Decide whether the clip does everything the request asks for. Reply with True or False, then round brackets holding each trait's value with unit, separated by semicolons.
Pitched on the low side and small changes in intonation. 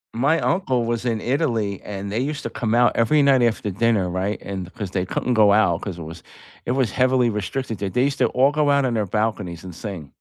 False (115 Hz; 4.6 semitones)